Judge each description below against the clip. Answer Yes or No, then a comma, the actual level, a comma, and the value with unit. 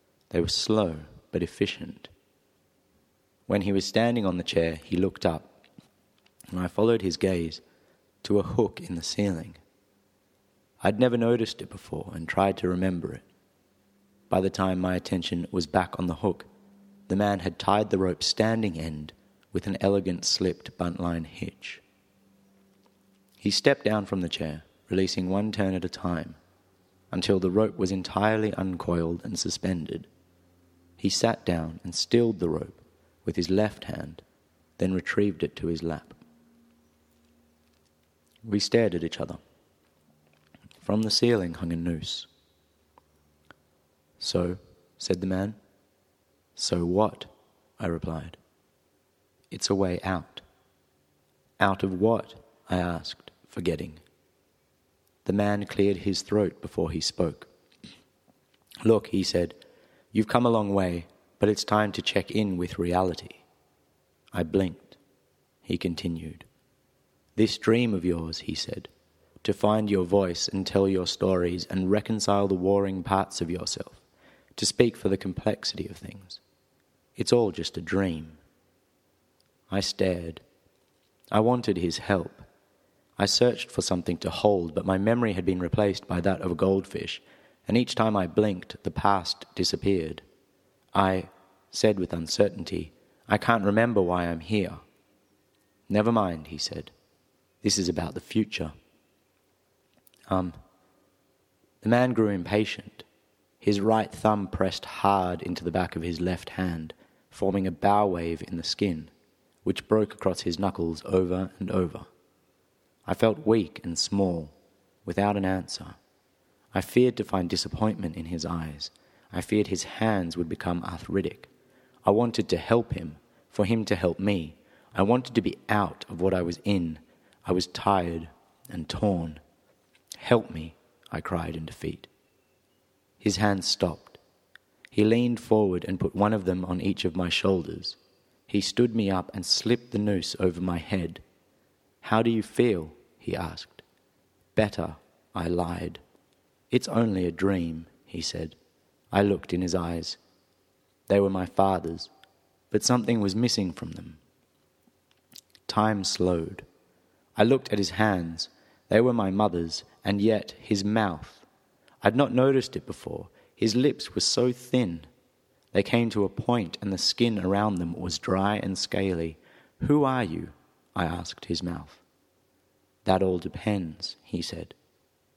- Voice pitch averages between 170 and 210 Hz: No, very low, 95 Hz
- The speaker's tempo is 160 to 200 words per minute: No, average, 145 wpm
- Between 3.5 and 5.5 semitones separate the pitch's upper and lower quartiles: No, average, 3.1 semitones